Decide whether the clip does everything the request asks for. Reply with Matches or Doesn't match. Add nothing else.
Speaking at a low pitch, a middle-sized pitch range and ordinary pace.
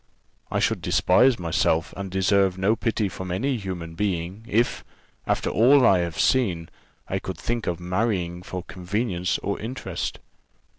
Matches